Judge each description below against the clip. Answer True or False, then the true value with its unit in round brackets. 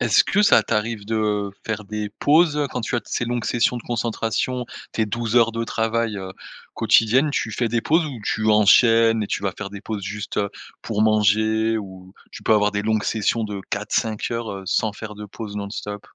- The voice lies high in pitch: False (110 Hz)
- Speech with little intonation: True (2.1 semitones)